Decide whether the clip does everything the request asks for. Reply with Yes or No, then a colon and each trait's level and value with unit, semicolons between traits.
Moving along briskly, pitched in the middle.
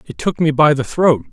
Yes: fast, 275 wpm; medium, 150 Hz